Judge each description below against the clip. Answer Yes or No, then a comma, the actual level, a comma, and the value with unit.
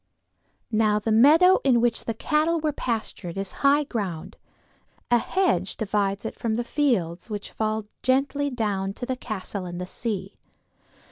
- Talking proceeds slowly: No, average, 155 wpm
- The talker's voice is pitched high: Yes, high, 225 Hz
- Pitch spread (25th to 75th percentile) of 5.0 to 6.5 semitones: Yes, average, 5.3 semitones